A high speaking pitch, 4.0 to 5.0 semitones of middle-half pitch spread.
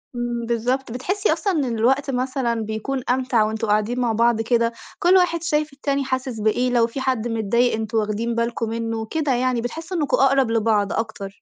No: high, 240 Hz; average, 3.1 semitones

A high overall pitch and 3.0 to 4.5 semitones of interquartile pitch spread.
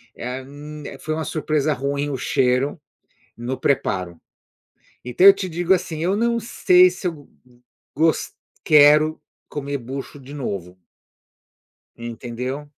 No: medium, 145 Hz; average, 3.9 semitones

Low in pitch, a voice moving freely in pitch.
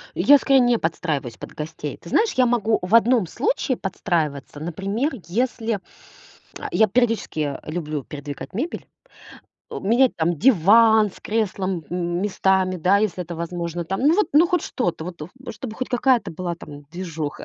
No: high, 190 Hz; wide, 6.0 semitones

